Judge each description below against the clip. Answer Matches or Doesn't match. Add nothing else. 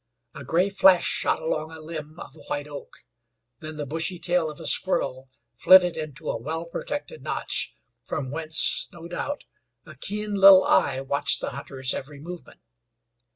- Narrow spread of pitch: Doesn't match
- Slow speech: Doesn't match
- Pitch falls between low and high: Matches